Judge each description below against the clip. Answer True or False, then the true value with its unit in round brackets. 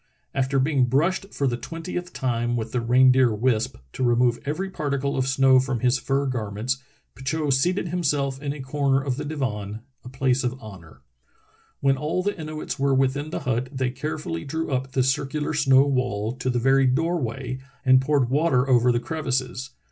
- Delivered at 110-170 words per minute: False (185 wpm)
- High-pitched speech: False (130 Hz)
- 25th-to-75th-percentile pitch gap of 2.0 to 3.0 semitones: True (2.7 semitones)